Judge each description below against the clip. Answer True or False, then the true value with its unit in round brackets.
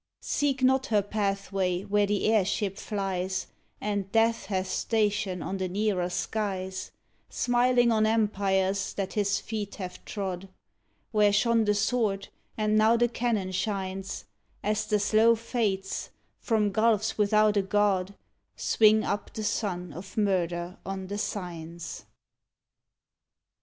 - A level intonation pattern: True (2.2 semitones)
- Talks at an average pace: False (130 wpm)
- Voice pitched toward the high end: True (205 Hz)